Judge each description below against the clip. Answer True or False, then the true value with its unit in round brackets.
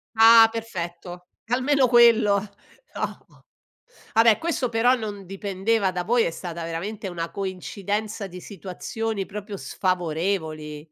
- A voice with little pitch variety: False (4.0 semitones)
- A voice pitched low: False (200 Hz)